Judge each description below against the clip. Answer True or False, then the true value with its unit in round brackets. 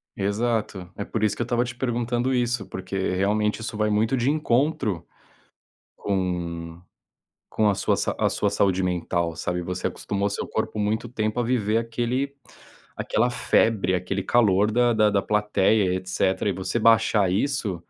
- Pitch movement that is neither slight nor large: True (4.0 semitones)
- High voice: False (105 Hz)